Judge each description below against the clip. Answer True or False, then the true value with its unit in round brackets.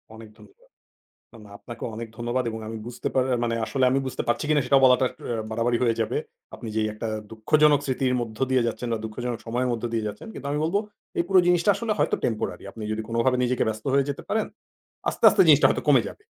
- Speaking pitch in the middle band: False (120 Hz)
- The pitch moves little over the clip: False (3.2 semitones)